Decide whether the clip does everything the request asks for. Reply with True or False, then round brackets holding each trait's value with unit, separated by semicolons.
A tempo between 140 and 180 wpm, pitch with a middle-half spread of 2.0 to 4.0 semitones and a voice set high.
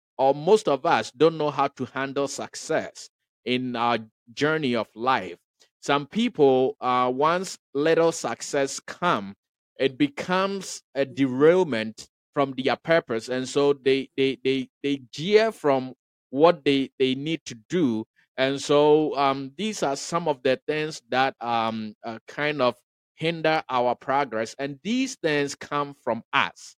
False (150 wpm; 3.3 semitones; 140 Hz)